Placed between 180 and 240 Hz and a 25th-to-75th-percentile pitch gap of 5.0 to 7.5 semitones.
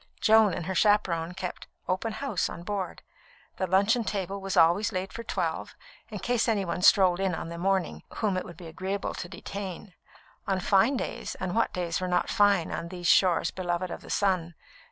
No: high, 190 Hz; narrow, 2.5 semitones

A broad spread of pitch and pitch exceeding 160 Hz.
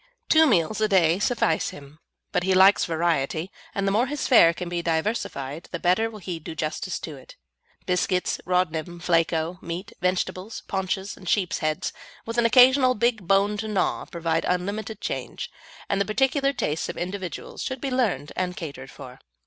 No: average, 4.4 semitones; medium, 185 Hz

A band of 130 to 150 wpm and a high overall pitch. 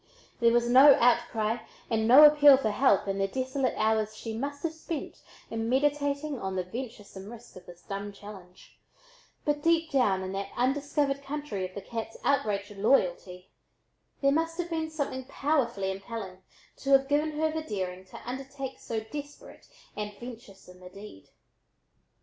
No: average, 160 wpm; high, 240 Hz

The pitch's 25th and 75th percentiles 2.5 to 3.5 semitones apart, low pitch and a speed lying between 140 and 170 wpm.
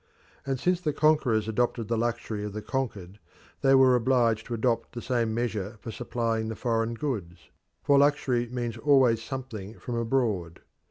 Yes: average, 2.9 semitones; low, 115 Hz; average, 165 wpm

